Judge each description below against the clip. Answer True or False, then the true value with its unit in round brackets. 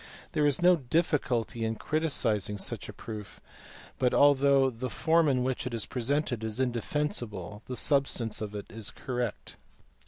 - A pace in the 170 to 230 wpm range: True (175 wpm)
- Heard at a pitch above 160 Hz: False (125 Hz)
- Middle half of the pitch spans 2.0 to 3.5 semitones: False (4.3 semitones)